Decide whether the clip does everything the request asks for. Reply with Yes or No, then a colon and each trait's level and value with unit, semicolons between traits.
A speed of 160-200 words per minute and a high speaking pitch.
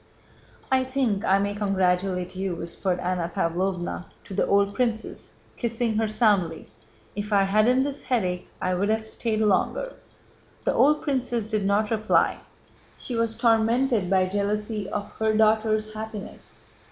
No: average, 140 wpm; high, 210 Hz